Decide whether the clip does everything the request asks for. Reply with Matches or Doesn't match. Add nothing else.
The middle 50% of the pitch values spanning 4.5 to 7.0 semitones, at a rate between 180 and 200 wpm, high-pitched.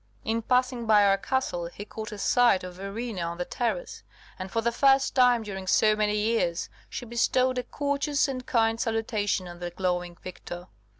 Matches